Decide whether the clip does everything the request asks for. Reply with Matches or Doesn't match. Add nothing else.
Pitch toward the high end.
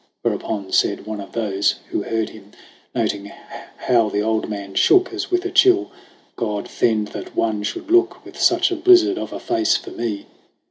Doesn't match